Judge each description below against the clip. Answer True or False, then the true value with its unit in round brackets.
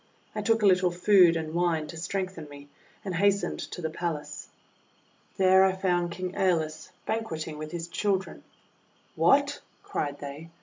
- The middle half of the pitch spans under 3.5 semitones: True (3.1 semitones)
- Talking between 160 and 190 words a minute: False (150 wpm)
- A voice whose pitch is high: False (175 Hz)